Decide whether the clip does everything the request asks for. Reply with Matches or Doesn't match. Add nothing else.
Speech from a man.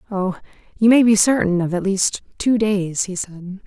Doesn't match